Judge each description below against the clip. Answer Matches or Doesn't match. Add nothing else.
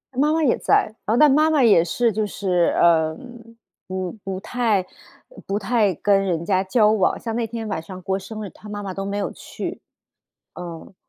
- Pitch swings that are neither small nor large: Matches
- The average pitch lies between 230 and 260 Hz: Doesn't match